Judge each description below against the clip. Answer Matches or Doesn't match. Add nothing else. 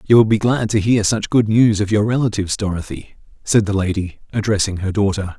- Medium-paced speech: Doesn't match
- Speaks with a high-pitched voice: Doesn't match